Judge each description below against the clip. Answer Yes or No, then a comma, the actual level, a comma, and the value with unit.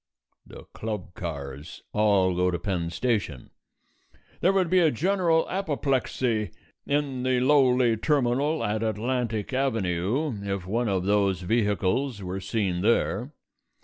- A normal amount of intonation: No, wide, 5.9 semitones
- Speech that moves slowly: Yes, slow, 125 wpm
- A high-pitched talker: No, low, 110 Hz